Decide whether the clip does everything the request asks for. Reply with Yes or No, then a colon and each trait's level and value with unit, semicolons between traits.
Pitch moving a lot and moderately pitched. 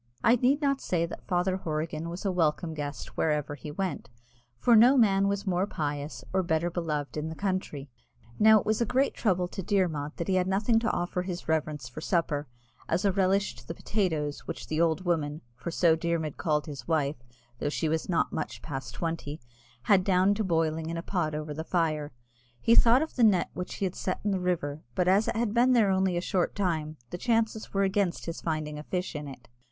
No: average, 4.0 semitones; medium, 175 Hz